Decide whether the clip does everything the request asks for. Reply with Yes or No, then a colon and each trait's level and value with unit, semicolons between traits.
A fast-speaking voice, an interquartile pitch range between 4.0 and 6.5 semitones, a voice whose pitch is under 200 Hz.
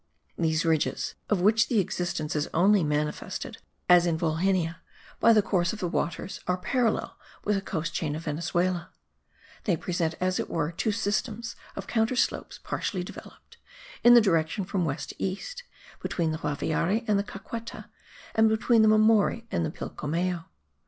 No: average, 165 wpm; average, 4.7 semitones; medium, 185 Hz